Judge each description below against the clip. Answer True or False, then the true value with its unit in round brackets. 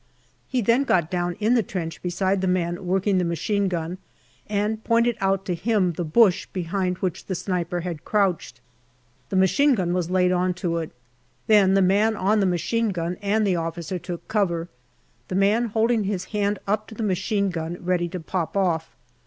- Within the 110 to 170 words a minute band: False (190 wpm)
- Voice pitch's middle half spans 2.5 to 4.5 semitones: True (3.0 semitones)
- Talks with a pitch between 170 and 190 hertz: True (185 Hz)